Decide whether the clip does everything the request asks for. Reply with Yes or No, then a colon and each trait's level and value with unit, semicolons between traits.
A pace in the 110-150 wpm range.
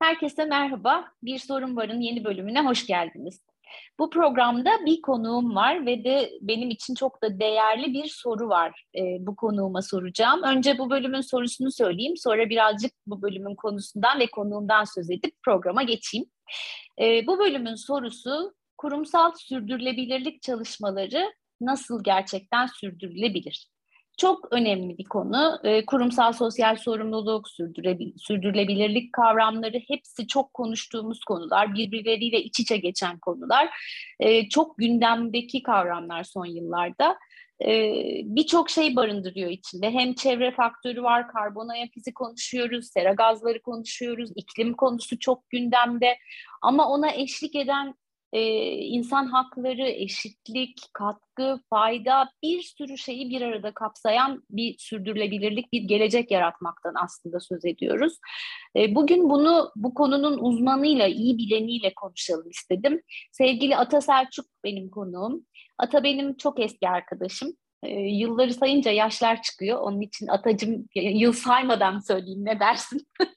Yes: average, 125 wpm